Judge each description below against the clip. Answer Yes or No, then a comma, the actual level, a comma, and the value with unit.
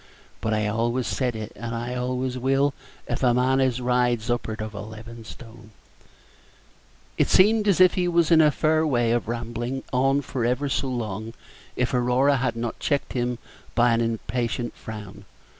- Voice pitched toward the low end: Yes, low, 120 Hz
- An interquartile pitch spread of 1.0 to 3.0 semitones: Yes, narrow, 2.5 semitones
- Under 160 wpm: No, average, 175 wpm